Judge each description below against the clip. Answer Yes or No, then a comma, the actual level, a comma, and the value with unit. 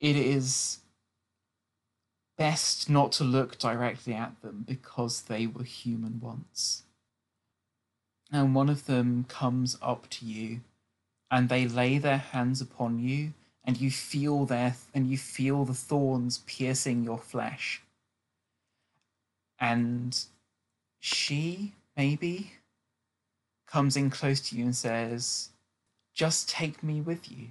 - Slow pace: Yes, slow, 125 wpm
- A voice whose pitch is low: Yes, low, 125 Hz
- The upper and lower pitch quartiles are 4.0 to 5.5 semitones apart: No, average, 3.0 semitones